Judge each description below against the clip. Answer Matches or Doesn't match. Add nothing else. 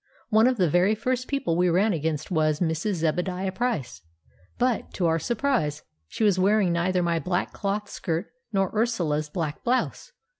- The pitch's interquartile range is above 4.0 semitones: Matches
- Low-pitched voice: Doesn't match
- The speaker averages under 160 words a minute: Doesn't match